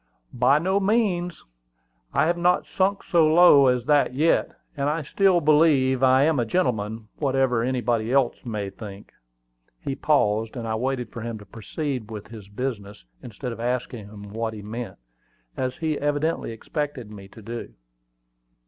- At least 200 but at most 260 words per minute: No, average, 165 wpm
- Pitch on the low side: Yes, low, 125 Hz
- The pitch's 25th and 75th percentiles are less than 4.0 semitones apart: No, average, 5.2 semitones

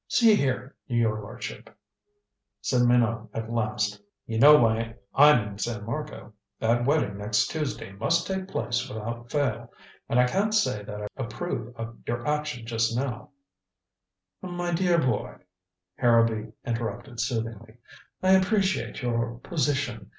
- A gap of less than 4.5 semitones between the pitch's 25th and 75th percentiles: No, average, 4.8 semitones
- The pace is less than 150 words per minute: Yes, average, 140 wpm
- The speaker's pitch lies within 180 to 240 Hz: No, low, 120 Hz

